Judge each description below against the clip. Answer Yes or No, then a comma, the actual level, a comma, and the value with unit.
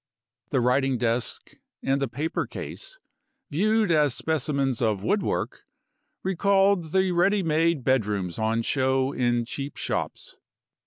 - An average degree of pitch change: No, wide, 6.1 semitones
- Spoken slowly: Yes, slow, 120 wpm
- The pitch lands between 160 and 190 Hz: No, medium, 140 Hz